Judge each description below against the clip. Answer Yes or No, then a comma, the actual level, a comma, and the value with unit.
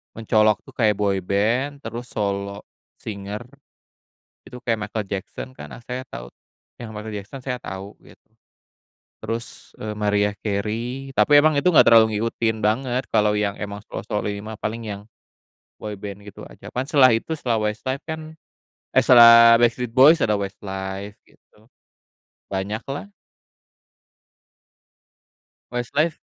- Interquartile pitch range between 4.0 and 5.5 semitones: No, average, 3.1 semitones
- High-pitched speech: No, low, 110 Hz